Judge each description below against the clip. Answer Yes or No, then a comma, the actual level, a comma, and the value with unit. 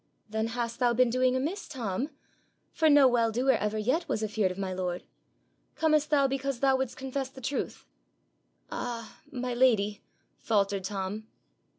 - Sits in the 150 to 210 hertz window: No, high, 245 Hz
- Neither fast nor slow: Yes, average, 160 wpm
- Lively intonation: No, average, 3.9 semitones